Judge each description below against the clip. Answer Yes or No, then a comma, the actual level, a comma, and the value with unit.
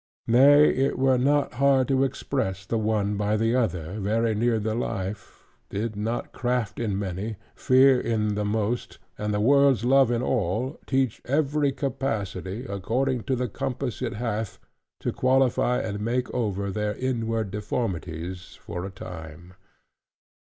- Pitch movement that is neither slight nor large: Yes, average, 4.1 semitones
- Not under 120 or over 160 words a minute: Yes, average, 150 wpm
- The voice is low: Yes, low, 115 Hz